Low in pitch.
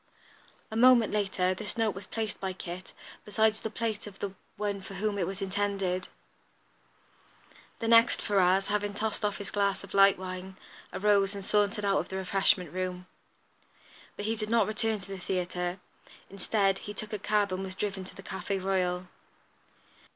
No: high, 200 Hz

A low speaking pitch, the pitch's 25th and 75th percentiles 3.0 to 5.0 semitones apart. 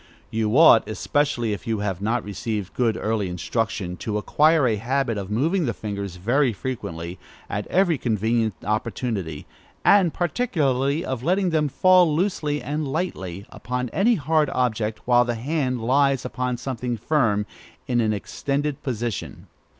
No: low, 125 Hz; wide, 5.6 semitones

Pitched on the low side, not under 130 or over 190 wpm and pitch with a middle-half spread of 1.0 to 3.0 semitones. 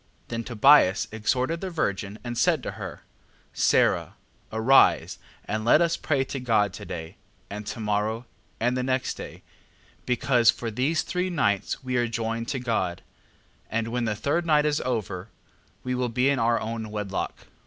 No: low, 120 Hz; average, 175 wpm; average, 3.5 semitones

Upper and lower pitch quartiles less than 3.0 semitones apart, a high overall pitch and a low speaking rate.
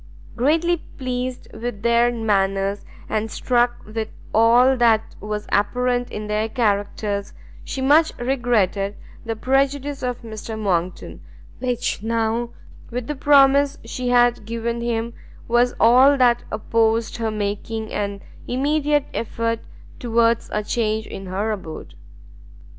Yes: narrow, 2.6 semitones; high, 230 Hz; slow, 125 wpm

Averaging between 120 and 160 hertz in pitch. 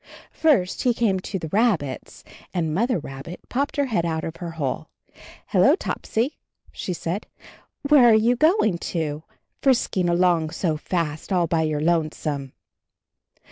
No: medium, 175 Hz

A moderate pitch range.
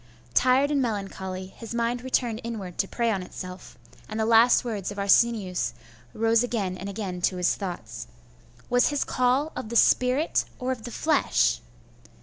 Yes: average, 4.4 semitones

